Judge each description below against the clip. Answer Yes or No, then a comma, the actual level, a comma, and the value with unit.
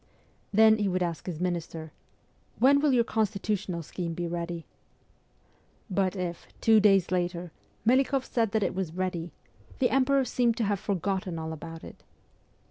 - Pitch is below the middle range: No, high, 190 Hz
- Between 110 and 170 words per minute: Yes, average, 165 wpm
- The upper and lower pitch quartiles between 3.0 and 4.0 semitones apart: No, average, 4.4 semitones